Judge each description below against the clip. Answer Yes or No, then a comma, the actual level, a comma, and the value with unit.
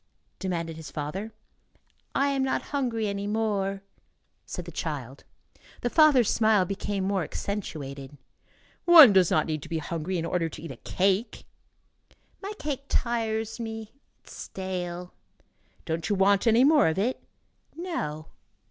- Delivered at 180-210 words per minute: No, average, 150 wpm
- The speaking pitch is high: Yes, high, 200 Hz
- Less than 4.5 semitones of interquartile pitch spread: No, wide, 5.5 semitones